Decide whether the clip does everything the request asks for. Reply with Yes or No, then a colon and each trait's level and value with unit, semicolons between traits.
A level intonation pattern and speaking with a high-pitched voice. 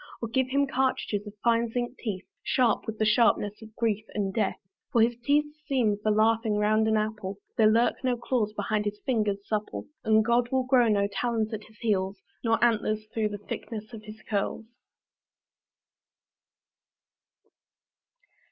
Yes: narrow, 2.1 semitones; high, 220 Hz